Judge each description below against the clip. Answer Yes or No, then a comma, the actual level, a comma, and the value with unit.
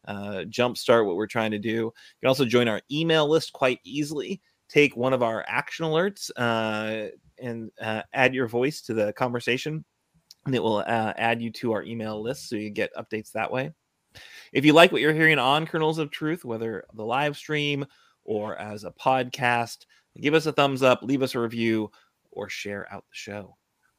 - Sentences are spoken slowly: No, average, 200 wpm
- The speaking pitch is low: Yes, low, 120 Hz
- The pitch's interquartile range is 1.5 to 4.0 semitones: No, average, 4.8 semitones